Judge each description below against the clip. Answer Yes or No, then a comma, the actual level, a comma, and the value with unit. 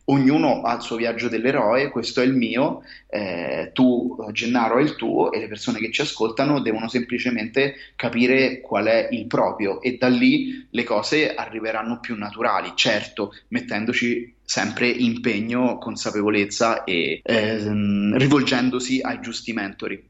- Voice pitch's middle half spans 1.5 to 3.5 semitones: Yes, narrow, 2.6 semitones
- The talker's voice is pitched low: Yes, low, 120 Hz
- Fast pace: No, average, 145 wpm